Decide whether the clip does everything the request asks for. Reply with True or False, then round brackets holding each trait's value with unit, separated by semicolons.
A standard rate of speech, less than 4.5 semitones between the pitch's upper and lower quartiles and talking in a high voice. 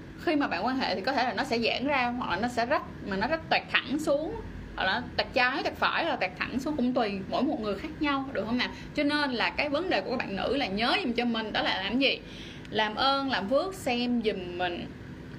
False (275 wpm; 3.8 semitones; 255 Hz)